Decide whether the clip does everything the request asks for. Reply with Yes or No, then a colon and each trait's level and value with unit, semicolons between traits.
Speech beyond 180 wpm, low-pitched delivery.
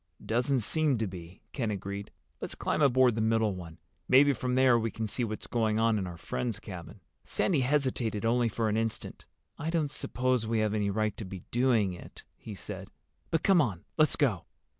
Yes: average, 200 wpm; low, 115 Hz